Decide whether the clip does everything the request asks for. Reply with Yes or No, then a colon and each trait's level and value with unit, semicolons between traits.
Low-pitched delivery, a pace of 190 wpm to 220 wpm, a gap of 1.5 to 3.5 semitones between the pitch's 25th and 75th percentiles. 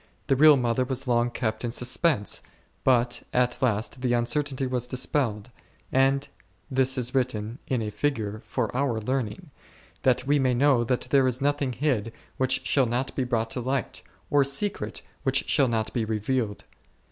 No: low, 125 Hz; average, 170 wpm; narrow, 2.5 semitones